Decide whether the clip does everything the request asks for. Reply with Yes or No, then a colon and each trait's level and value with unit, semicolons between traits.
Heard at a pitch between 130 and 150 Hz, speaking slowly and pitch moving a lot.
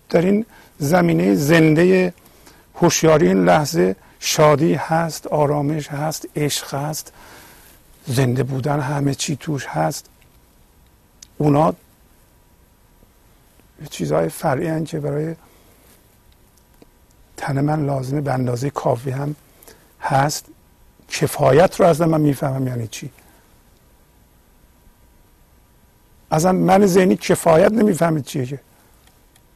Yes: medium, 140 Hz; slow, 95 wpm; wide, 8.6 semitones